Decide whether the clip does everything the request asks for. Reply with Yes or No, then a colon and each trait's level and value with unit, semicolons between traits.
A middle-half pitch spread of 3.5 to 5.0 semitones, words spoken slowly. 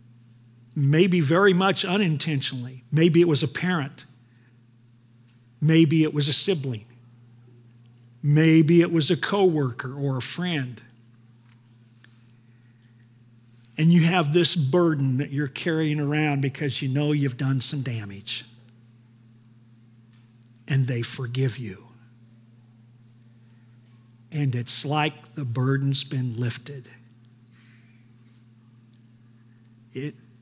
Yes: average, 3.9 semitones; slow, 100 wpm